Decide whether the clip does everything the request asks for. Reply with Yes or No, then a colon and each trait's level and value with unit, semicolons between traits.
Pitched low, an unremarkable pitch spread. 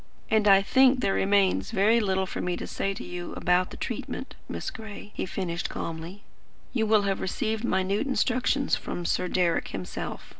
No: high, 195 Hz; average, 3.4 semitones